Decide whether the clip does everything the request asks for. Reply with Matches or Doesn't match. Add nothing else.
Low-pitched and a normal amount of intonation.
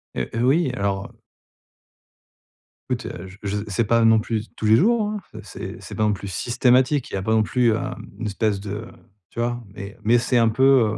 Matches